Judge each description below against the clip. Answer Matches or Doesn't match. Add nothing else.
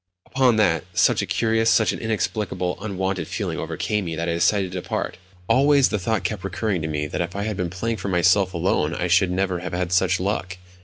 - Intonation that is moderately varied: Matches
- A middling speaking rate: Doesn't match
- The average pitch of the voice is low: Matches